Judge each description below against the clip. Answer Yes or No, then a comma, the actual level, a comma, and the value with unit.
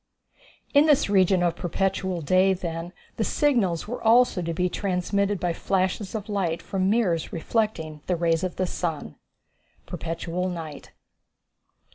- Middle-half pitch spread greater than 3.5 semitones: No, average, 3.1 semitones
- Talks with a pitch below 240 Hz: Yes, medium, 185 Hz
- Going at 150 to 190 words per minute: No, average, 140 wpm